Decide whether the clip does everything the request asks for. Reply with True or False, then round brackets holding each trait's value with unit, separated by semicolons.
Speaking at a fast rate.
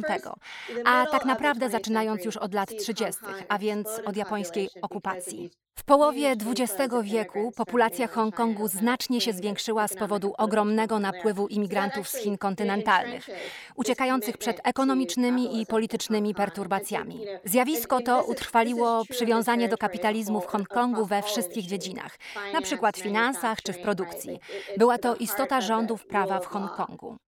False (135 wpm)